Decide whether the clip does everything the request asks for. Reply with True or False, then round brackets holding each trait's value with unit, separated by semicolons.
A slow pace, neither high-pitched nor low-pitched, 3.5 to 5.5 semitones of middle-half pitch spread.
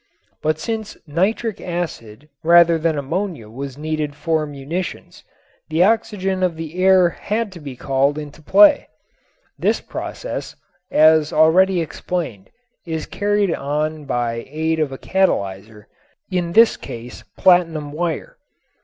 True (125 wpm; 160 Hz; 4.1 semitones)